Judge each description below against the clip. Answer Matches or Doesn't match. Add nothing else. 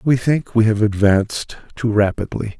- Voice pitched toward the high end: Doesn't match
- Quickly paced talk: Doesn't match